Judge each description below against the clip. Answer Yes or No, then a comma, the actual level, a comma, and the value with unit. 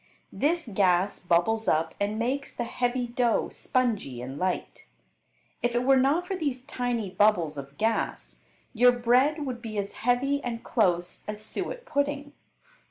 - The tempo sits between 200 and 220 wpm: No, average, 155 wpm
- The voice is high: Yes, high, 235 Hz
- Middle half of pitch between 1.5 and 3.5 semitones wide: No, average, 4.4 semitones